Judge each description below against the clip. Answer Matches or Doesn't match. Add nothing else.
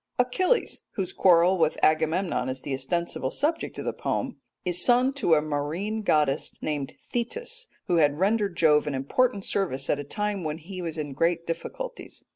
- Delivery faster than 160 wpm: Matches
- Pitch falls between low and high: Matches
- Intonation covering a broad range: Matches